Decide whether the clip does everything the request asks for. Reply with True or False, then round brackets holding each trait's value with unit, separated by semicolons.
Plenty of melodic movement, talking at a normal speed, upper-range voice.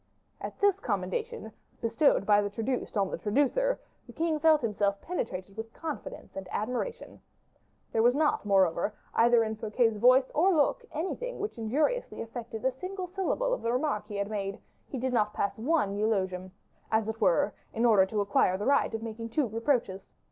True (6.7 semitones; 180 wpm; 230 Hz)